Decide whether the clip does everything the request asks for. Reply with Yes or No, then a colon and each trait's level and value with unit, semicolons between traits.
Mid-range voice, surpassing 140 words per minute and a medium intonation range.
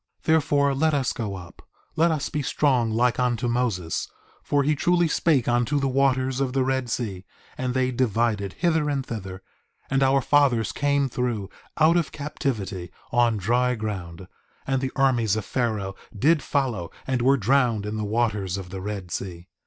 No: low, 125 Hz; average, 175 wpm; average, 4.7 semitones